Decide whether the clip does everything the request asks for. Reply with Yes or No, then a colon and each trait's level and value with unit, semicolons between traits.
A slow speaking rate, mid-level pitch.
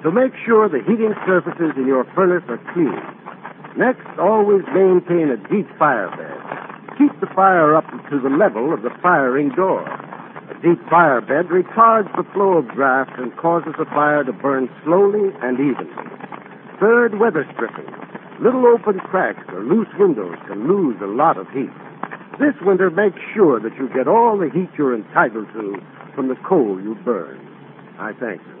No: average, 175 wpm; medium, 180 Hz